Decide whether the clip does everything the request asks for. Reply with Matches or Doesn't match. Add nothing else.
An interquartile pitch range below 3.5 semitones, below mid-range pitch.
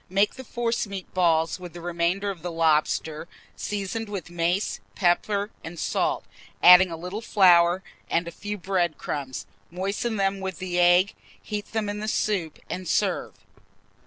Doesn't match